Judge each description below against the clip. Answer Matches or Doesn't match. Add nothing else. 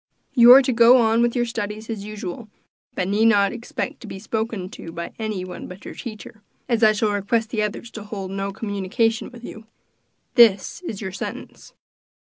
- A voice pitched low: Doesn't match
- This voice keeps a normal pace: Matches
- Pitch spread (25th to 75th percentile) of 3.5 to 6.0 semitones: Doesn't match